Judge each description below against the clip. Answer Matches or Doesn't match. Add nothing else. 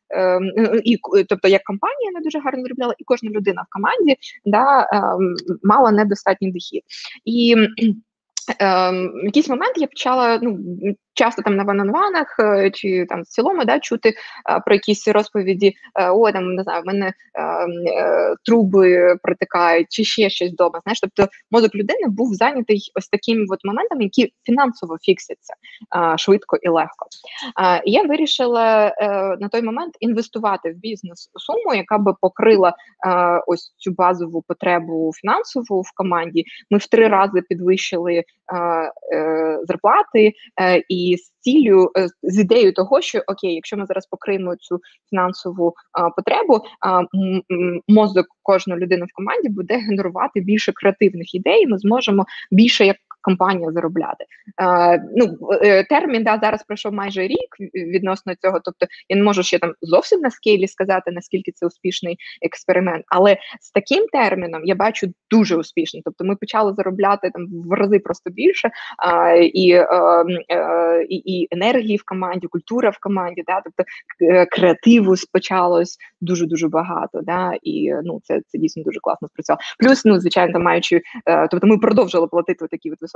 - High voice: Matches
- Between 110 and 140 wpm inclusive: Doesn't match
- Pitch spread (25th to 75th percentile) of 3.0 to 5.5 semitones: Matches